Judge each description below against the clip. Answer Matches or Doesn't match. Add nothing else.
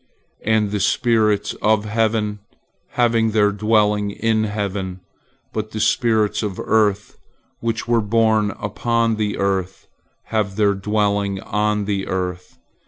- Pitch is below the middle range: Matches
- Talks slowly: Matches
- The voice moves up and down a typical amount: Doesn't match